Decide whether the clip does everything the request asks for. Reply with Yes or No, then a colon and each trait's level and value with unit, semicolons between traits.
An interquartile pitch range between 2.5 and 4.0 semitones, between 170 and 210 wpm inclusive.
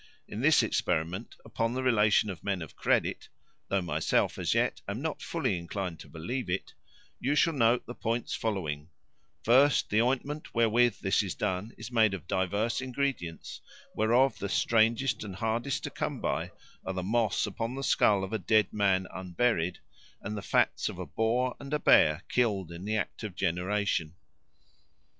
No: average, 4.5 semitones; average, 175 wpm